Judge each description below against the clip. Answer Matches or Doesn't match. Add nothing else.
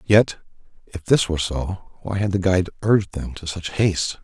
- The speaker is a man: Matches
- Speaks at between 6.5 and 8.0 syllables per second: Doesn't match